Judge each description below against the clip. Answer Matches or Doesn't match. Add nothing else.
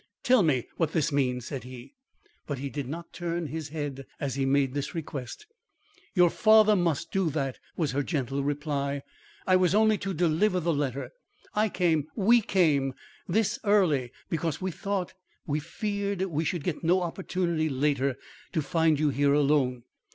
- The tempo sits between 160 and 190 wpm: Matches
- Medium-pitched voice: Matches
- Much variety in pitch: Doesn't match